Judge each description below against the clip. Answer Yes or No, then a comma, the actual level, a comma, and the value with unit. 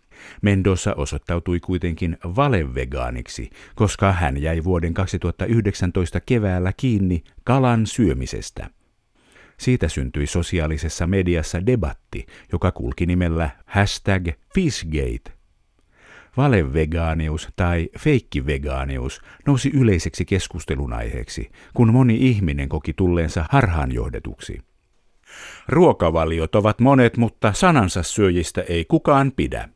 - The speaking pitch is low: Yes, very low, 90 Hz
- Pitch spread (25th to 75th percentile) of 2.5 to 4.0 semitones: No, average, 5.0 semitones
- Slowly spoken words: Yes, slow, 90 wpm